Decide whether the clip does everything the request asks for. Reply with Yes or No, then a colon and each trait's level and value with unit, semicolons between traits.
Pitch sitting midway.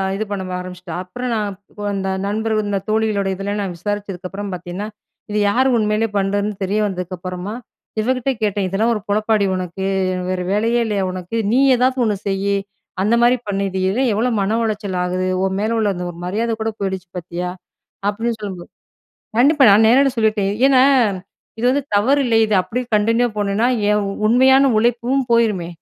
No: high, 210 Hz